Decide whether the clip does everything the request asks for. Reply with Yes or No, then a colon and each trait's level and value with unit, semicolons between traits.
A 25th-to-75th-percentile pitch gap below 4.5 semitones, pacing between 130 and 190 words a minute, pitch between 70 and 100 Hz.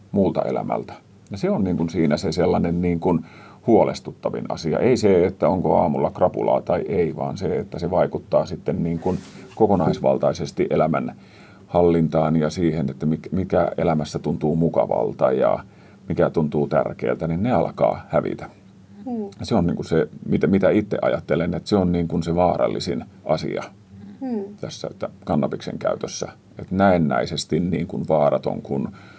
Yes: narrow, 2.6 semitones; fast, 155 wpm; very low, 85 Hz